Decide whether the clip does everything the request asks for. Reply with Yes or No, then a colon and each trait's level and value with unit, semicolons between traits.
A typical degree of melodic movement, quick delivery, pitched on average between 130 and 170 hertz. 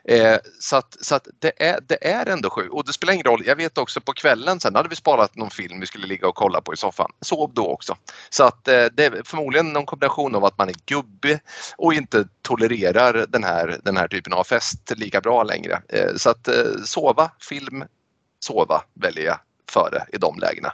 No: wide, 7.9 semitones; fast, 225 wpm; medium, 140 Hz